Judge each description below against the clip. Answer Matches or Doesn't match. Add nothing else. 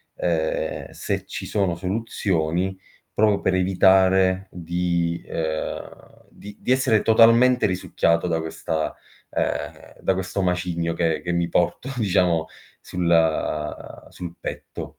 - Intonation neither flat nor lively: Matches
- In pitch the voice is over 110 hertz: Doesn't match